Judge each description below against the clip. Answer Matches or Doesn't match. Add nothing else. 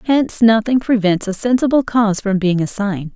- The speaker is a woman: Matches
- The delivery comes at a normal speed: Matches